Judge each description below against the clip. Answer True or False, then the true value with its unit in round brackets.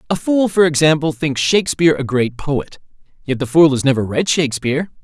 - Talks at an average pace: True (190 wpm)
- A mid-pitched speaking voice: True (145 Hz)